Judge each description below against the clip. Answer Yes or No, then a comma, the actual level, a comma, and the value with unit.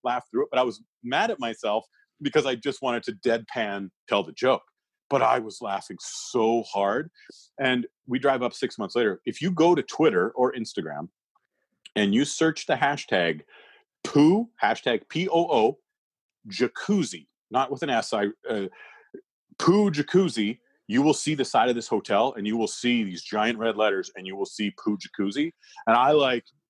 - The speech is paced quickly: No, average, 180 wpm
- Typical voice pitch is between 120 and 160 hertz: Yes, medium, 140 Hz